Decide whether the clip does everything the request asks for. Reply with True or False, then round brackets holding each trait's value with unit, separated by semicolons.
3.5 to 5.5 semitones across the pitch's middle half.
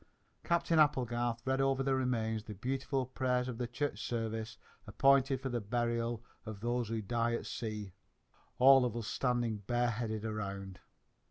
False (2.7 semitones)